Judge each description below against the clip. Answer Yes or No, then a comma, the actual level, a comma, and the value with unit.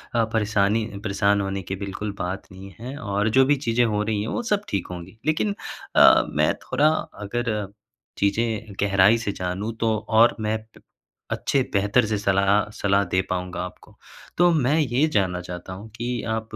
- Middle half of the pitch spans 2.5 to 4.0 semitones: Yes, average, 2.8 semitones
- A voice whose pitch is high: No, low, 105 Hz